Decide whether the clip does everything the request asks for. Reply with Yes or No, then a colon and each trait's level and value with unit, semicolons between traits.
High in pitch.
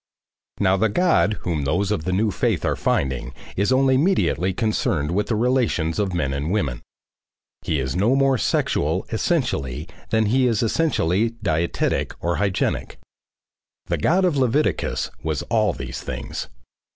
No: low, 100 Hz